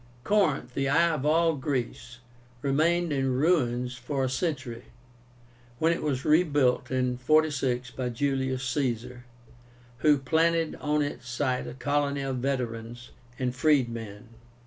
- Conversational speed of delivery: No, slow, 130 wpm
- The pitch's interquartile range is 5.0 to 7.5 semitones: No, average, 3.3 semitones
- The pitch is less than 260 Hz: Yes, low, 135 Hz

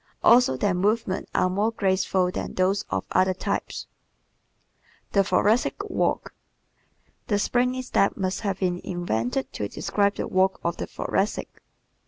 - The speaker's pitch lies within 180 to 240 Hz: Yes, high, 190 Hz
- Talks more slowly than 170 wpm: Yes, average, 145 wpm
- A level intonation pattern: Yes, narrow, 2.2 semitones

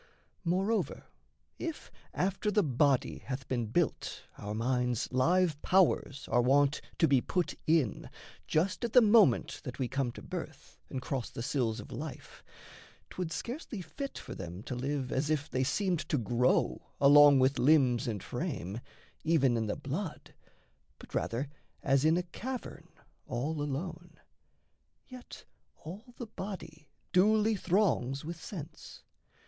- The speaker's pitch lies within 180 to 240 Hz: No, medium, 145 Hz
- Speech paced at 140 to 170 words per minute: Yes, average, 145 wpm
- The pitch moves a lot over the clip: Yes, wide, 6.1 semitones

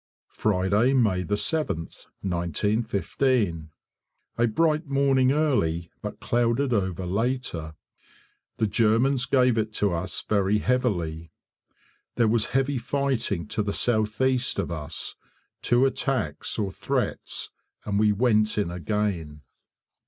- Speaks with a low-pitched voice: Yes, low, 110 Hz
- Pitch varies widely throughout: Yes, wide, 5.7 semitones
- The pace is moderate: No, slow, 115 wpm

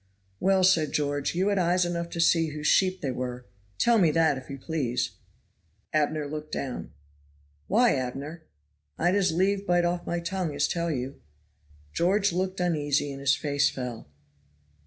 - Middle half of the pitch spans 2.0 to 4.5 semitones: Yes, average, 4.0 semitones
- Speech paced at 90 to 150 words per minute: No, average, 165 wpm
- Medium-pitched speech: Yes, medium, 165 Hz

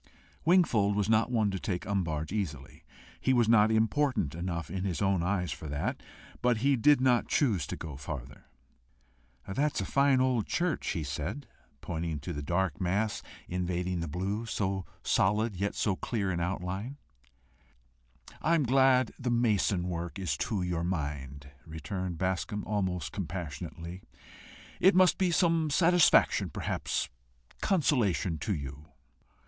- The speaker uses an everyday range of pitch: No, wide, 5.9 semitones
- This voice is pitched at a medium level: No, very low, 95 Hz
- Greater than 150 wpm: No, average, 145 wpm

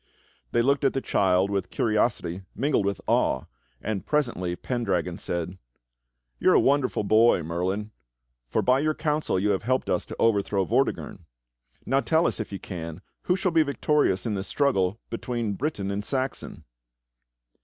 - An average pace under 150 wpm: No, average, 165 wpm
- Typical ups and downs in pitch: No, wide, 6.2 semitones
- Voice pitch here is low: Yes, low, 105 Hz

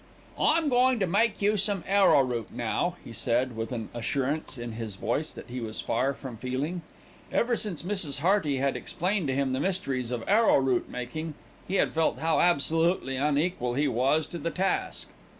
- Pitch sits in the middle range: Yes, medium, 145 Hz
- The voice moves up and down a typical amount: No, wide, 6.5 semitones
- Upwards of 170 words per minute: Yes, average, 180 wpm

